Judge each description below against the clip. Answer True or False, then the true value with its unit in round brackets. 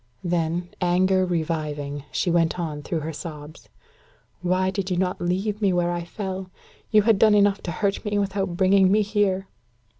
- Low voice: False (185 Hz)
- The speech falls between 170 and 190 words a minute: True (175 wpm)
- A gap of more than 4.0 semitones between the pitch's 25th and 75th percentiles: False (2.6 semitones)